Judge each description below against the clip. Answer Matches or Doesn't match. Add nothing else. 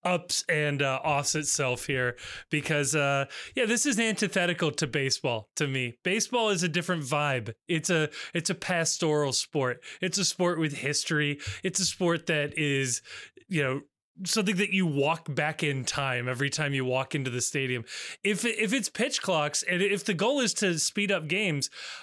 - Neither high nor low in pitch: Matches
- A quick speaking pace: Doesn't match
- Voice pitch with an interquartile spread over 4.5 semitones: Matches